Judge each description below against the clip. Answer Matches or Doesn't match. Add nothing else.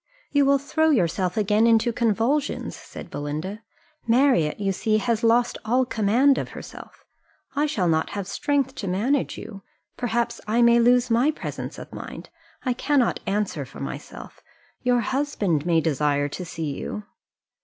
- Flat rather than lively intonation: Doesn't match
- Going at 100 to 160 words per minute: Matches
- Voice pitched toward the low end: Doesn't match